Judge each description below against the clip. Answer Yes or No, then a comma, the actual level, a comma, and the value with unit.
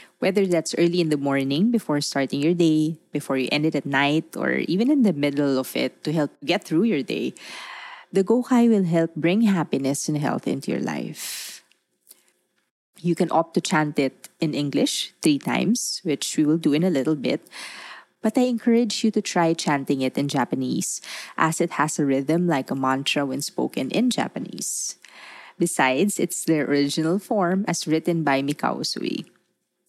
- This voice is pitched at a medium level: Yes, medium, 160 Hz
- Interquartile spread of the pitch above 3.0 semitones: Yes, average, 5.2 semitones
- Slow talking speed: No, average, 180 wpm